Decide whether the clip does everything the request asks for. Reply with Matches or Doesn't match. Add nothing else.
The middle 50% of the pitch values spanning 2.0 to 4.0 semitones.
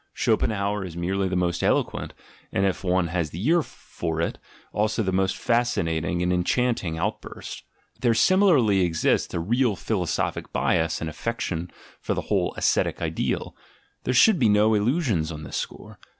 Doesn't match